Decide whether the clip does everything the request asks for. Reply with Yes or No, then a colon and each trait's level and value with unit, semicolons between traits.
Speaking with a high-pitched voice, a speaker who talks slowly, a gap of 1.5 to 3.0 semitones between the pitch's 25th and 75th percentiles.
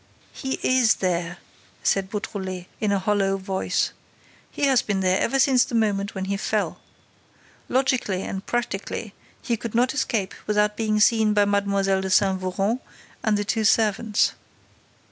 No: high, 205 Hz; average, 155 wpm; average, 2.7 semitones